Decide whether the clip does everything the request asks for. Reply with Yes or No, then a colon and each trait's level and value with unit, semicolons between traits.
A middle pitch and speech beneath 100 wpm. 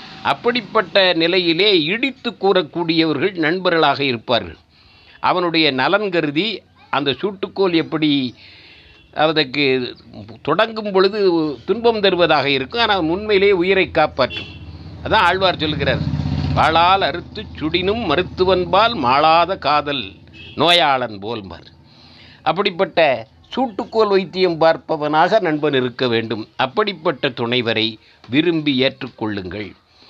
Yes: medium, 155 Hz; average, 90 wpm